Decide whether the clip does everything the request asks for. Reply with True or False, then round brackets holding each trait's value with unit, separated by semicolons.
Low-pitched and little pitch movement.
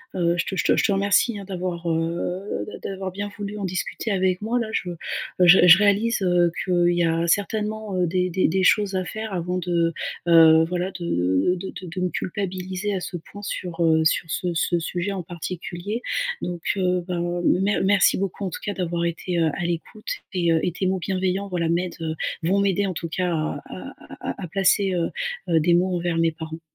False (180 Hz; 2.2 semitones)